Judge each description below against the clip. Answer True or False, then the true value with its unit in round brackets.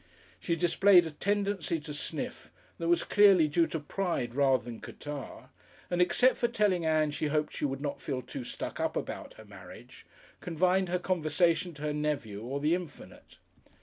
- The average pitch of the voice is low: False (160 Hz)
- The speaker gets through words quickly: False (180 wpm)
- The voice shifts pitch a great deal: False (3.7 semitones)